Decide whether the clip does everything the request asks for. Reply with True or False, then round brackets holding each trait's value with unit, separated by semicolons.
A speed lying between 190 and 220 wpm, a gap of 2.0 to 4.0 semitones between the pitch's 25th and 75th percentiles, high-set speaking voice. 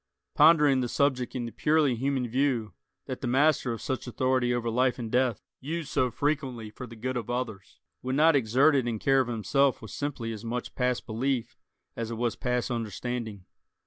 False (195 wpm; 2.6 semitones; 125 Hz)